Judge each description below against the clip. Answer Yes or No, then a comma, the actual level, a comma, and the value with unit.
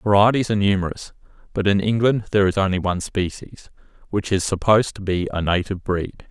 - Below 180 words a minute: No, average, 190 wpm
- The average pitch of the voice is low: Yes, low, 100 Hz